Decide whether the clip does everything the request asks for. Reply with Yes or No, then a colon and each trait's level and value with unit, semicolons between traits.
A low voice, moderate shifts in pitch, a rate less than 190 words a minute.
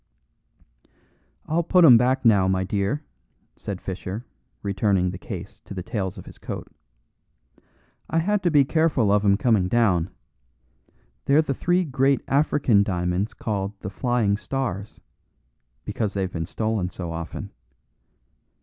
No: low, 105 Hz; wide, 6.0 semitones; average, 140 wpm